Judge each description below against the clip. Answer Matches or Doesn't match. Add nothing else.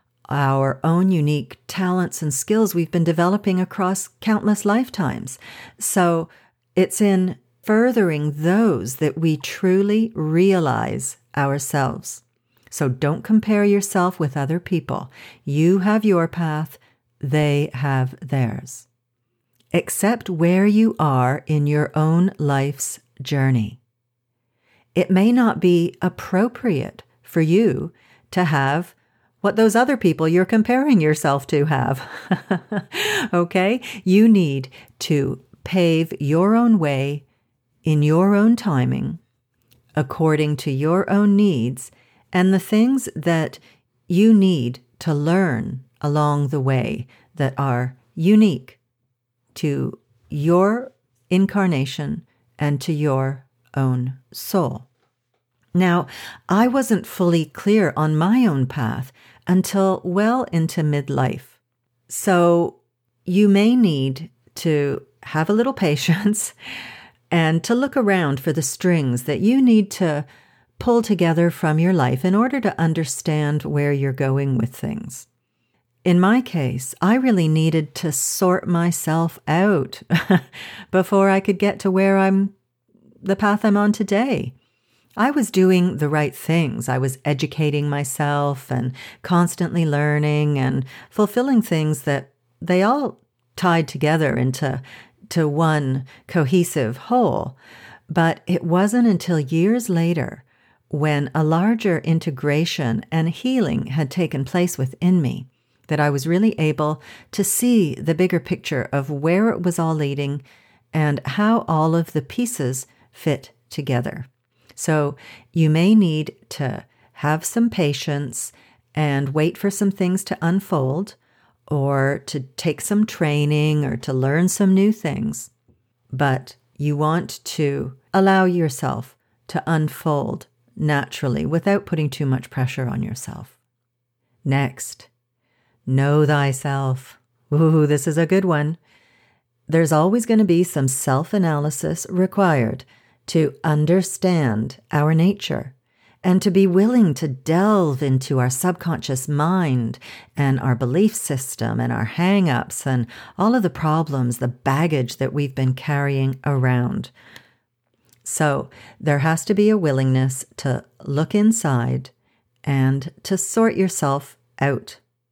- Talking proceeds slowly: Matches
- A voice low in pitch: Doesn't match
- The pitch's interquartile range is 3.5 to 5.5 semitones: Doesn't match